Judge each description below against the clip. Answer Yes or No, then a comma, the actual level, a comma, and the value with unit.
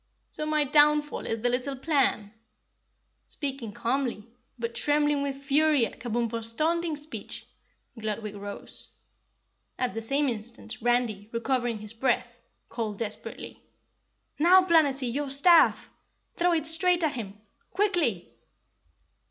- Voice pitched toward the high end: Yes, very high, 265 Hz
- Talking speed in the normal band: No, slow, 125 wpm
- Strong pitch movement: No, average, 4.7 semitones